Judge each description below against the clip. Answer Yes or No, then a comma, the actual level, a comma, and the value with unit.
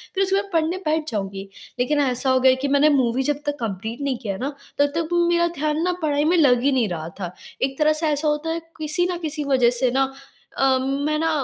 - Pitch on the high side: Yes, very high, 285 Hz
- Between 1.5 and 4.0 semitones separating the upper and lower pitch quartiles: Yes, average, 3.7 semitones